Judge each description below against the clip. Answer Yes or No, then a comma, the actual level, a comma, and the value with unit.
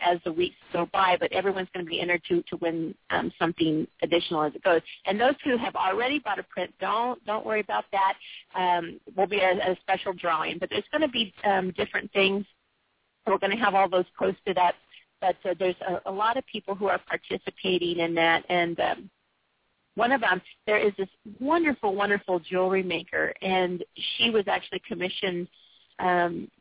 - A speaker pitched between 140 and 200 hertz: Yes, high, 190 Hz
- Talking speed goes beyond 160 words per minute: Yes, average, 195 wpm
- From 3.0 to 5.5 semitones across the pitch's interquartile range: No, narrow, 2.6 semitones